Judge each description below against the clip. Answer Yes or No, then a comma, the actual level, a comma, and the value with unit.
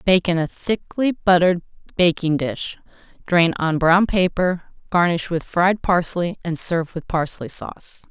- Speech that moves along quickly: No, average, 150 wpm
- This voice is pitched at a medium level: Yes, medium, 175 Hz